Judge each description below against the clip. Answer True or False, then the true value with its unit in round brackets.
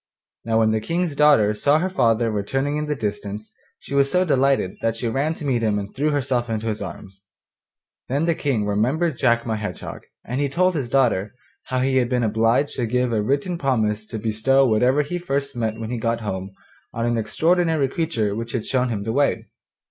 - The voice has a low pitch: True (125 Hz)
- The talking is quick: True (210 wpm)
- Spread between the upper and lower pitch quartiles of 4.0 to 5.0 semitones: True (4.4 semitones)